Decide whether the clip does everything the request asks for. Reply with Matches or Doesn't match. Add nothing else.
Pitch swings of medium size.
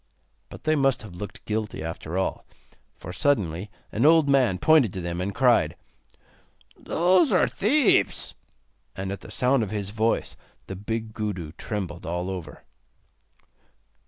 Doesn't match